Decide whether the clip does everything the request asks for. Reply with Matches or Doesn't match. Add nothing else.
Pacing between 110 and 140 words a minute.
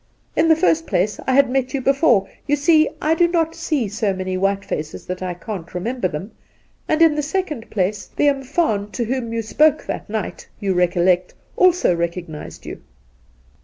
Doesn't match